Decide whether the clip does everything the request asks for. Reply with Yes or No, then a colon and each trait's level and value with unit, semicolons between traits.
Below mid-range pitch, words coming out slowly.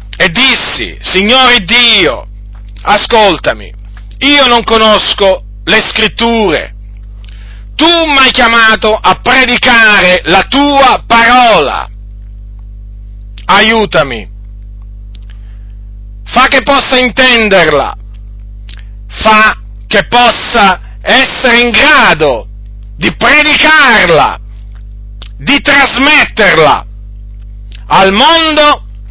No: high, 195 Hz; slow, 75 wpm